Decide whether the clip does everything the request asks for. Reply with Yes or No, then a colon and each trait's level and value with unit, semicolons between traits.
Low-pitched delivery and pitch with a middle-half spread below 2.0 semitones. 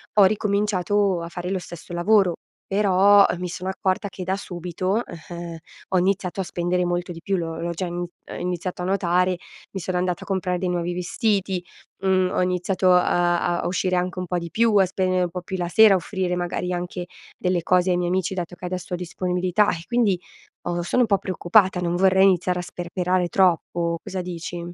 No: medium, 180 Hz; narrow, 1.4 semitones